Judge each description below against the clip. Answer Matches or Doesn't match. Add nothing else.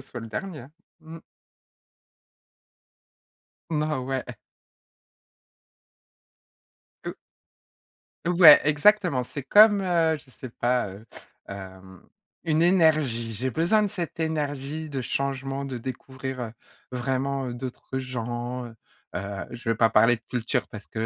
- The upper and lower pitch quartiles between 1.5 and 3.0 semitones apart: Doesn't match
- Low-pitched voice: Matches